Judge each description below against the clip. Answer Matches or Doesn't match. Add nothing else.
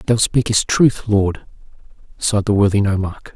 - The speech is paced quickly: Doesn't match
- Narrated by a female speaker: Doesn't match